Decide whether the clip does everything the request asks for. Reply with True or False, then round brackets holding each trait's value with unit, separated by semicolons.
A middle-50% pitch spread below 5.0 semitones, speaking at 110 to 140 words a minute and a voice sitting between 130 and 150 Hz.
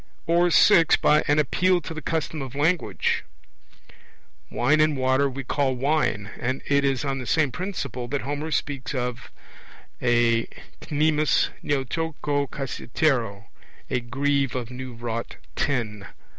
True (3.5 semitones; 135 wpm; 140 Hz)